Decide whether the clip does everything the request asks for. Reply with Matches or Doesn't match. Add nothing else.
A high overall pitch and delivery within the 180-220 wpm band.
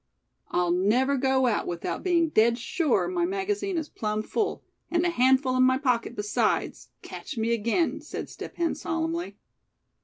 Doesn't match